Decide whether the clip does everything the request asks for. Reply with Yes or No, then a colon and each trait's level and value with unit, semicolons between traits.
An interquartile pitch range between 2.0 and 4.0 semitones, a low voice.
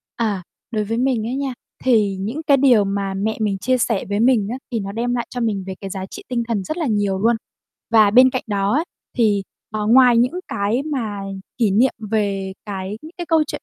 No: average, 3.7 semitones; high, 220 Hz